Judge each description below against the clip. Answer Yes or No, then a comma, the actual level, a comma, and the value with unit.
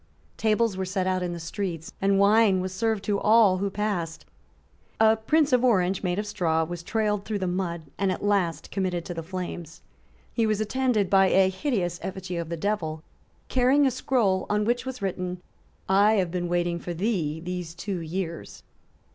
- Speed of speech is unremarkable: Yes, average, 190 wpm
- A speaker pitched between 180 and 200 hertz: Yes, high, 190 Hz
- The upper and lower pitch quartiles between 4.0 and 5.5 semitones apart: No, average, 3.3 semitones